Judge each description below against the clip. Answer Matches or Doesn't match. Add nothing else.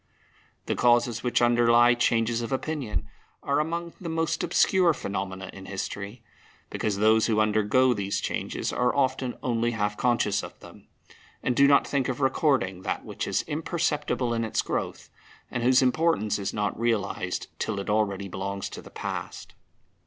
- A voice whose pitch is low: Matches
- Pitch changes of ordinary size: Matches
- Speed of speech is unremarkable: Matches